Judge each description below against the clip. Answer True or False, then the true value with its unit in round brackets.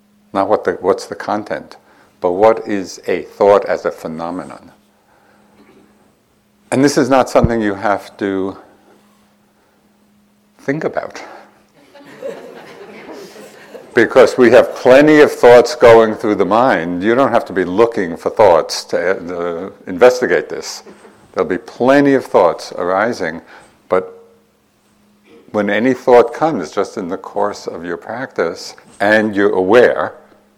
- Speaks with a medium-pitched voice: False (130 Hz)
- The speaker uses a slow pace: True (130 wpm)